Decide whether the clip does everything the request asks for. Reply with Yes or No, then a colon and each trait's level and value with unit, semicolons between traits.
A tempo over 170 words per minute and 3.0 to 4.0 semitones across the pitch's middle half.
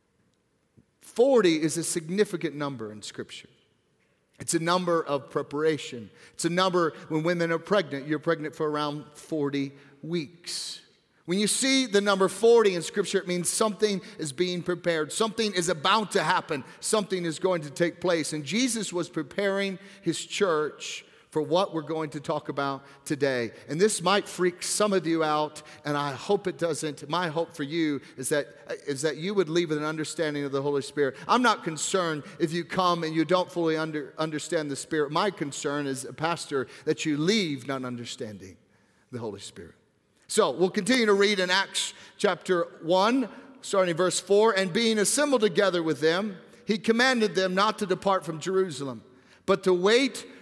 No: average, 180 wpm; average, 4.5 semitones